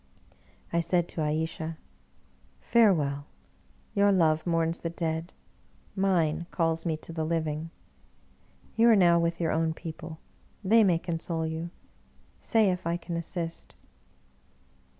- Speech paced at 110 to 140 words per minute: Yes, slow, 135 wpm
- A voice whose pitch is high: No, medium, 165 Hz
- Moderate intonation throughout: No, narrow, 1.5 semitones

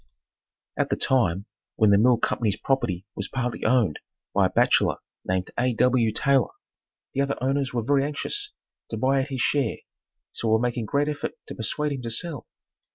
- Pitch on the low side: Yes, low, 125 Hz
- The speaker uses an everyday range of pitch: Yes, average, 3.7 semitones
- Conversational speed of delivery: Yes, average, 180 wpm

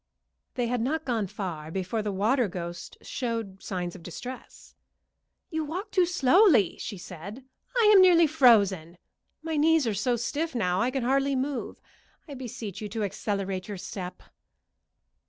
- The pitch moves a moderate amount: No, wide, 6.6 semitones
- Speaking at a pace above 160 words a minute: No, average, 155 wpm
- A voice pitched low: No, high, 235 Hz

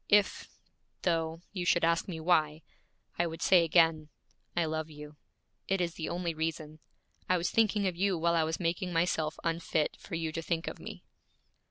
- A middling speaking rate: Yes, average, 185 wpm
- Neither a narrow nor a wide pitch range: No, narrow, 1.7 semitones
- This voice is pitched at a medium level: Yes, medium, 165 Hz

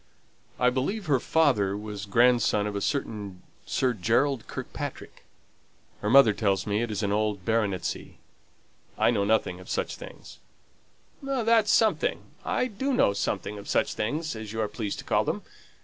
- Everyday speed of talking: Yes, average, 165 wpm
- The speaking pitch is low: Yes, low, 110 Hz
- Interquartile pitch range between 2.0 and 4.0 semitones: No, average, 5.2 semitones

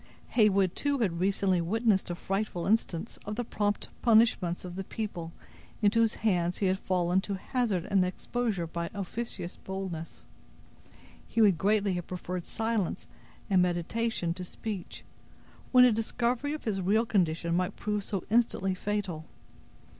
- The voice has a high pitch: Yes, high, 195 Hz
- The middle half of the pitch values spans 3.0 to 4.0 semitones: Yes, average, 3.7 semitones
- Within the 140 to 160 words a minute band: Yes, average, 155 wpm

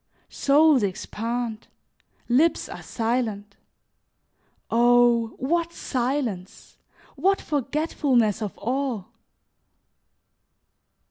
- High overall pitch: Yes, high, 245 Hz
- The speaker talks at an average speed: No, slow, 65 wpm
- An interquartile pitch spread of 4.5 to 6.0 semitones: No, average, 4.0 semitones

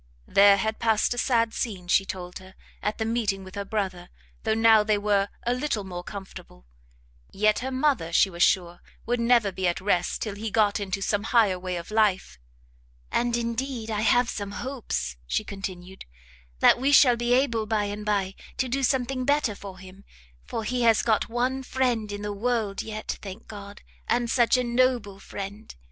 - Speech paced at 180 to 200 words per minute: Yes, average, 190 wpm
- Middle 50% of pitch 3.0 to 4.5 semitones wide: Yes, average, 3.5 semitones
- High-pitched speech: Yes, high, 215 Hz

